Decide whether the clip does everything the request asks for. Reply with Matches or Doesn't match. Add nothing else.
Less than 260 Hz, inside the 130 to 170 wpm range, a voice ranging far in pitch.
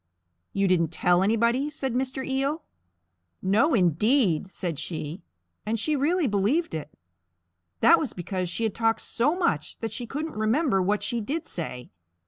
Matches